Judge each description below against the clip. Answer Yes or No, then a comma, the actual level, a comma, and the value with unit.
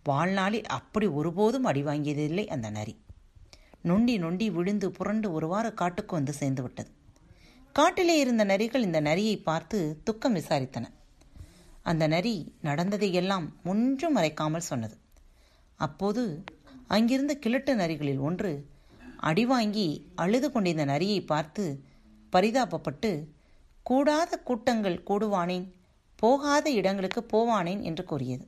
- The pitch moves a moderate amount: No, wide, 6.7 semitones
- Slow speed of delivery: No, average, 100 wpm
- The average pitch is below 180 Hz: No, medium, 185 Hz